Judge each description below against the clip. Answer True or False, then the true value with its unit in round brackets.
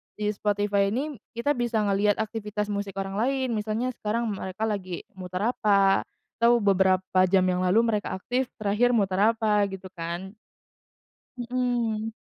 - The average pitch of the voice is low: False (210 Hz)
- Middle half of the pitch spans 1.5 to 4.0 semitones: True (3.1 semitones)